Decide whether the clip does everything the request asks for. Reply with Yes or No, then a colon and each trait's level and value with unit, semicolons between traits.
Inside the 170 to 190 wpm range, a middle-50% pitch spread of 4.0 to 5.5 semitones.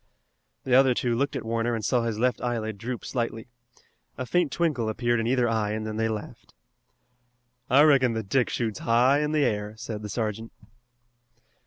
No: average, 185 wpm; average, 2.7 semitones